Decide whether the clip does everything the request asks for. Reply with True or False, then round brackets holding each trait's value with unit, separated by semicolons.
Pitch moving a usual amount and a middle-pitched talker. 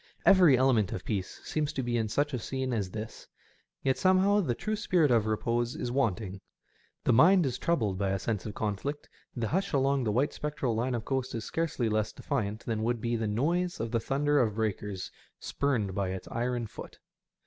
False (4.7 semitones; 120 Hz)